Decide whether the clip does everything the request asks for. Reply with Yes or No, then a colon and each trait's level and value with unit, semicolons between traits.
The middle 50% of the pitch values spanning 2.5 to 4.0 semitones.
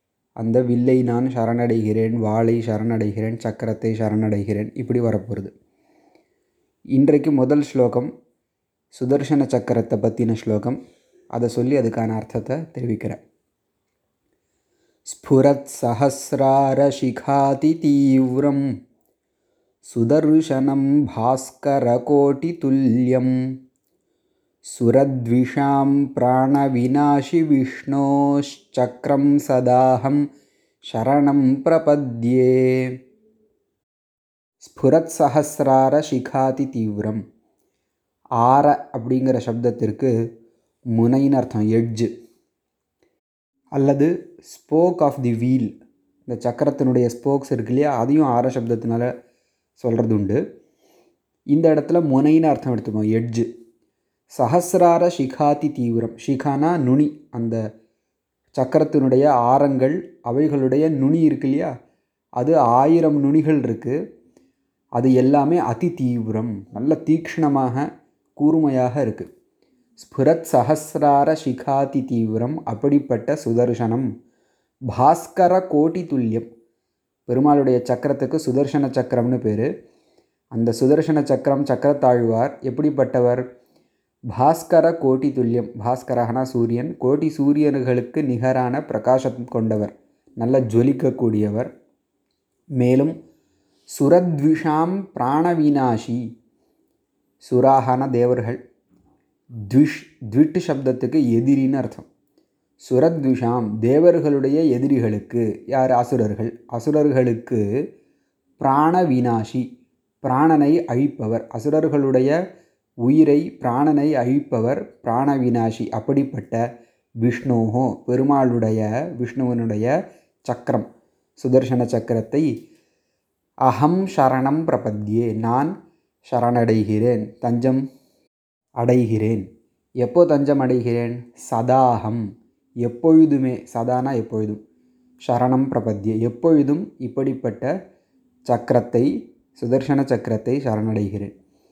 Yes: average, 3.5 semitones